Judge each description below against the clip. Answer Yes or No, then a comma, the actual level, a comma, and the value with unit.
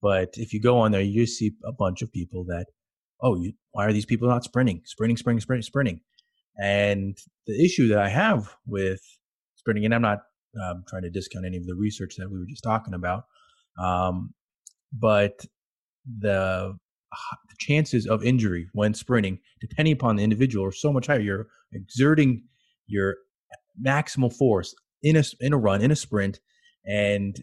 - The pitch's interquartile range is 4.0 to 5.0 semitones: Yes, average, 4.4 semitones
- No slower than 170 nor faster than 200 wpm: Yes, average, 175 wpm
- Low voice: Yes, low, 110 Hz